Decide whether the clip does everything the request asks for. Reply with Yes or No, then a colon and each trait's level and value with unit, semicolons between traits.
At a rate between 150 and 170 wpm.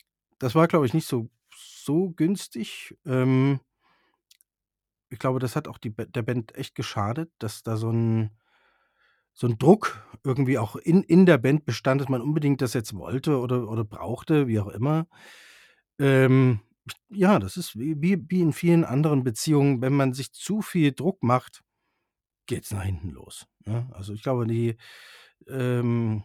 Yes: average, 165 wpm